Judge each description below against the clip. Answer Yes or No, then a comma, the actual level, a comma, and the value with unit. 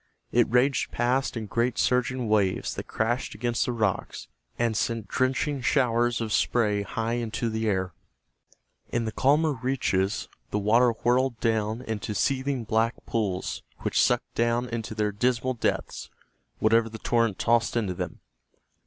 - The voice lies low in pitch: Yes, low, 115 Hz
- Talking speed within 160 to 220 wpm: No, average, 150 wpm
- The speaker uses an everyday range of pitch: No, narrow, 2.3 semitones